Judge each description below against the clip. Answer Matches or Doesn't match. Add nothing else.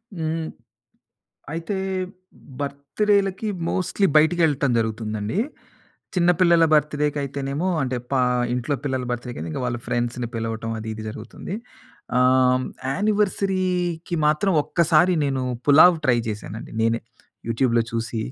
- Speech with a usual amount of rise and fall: Doesn't match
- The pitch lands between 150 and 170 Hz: Doesn't match